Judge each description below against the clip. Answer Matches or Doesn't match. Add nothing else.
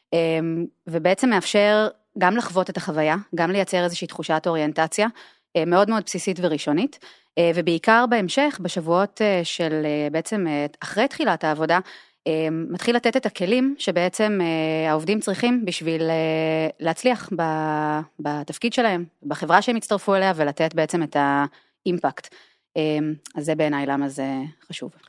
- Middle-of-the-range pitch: Matches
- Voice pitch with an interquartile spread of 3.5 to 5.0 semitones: Matches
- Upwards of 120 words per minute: Doesn't match